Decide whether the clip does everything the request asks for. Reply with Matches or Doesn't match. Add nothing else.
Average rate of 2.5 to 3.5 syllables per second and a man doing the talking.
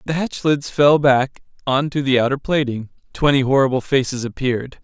Doesn't match